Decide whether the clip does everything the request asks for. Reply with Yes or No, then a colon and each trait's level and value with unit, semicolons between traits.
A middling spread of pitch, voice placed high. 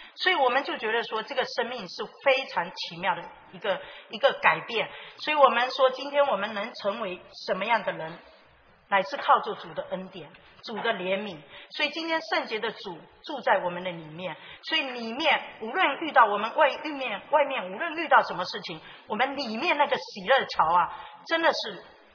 No: wide, 6.0 semitones; very high, 250 Hz